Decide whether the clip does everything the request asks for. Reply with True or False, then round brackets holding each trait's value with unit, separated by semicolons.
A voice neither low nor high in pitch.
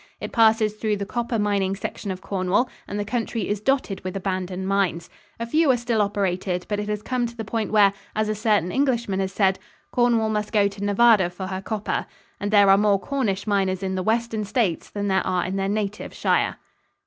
False (205 Hz)